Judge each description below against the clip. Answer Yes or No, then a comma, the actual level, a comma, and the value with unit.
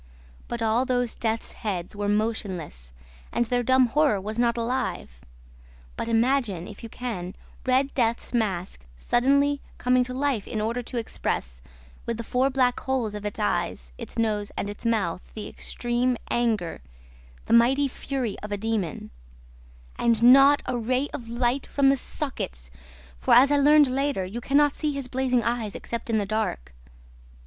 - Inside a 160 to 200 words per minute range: Yes, average, 170 wpm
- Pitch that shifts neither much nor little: Yes, average, 3.7 semitones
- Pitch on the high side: Yes, high, 235 Hz